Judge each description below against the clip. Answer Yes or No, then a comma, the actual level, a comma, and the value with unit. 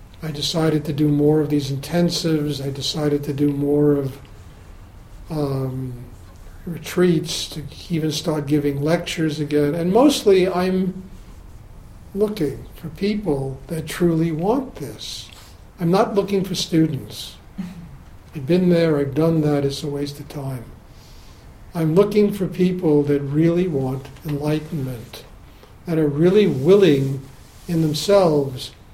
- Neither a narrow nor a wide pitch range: Yes, average, 4.0 semitones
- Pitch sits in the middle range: Yes, medium, 150 Hz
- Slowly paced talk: Yes, slow, 130 wpm